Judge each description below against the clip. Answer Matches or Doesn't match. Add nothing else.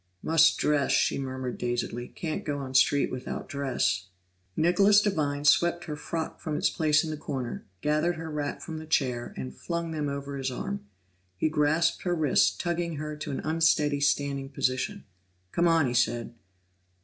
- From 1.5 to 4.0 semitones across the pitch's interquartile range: Matches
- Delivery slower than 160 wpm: Doesn't match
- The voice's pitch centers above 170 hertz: Doesn't match